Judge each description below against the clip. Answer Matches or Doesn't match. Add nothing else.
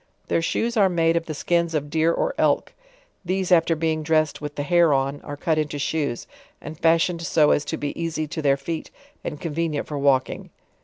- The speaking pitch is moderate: Matches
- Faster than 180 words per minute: Matches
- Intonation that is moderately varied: Doesn't match